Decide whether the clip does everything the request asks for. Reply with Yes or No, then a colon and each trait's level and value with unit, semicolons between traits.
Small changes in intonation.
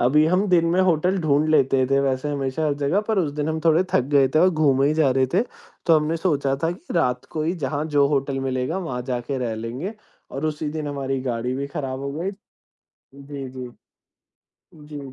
No: average, 3.1 semitones